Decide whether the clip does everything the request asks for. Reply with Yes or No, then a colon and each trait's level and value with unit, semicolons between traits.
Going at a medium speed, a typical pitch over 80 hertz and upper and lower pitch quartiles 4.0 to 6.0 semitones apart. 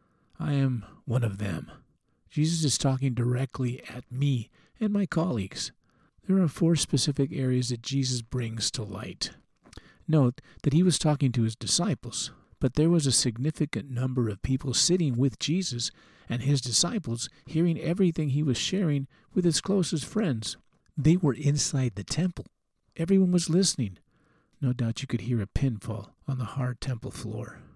Yes: average, 160 wpm; low, 135 Hz; average, 4.6 semitones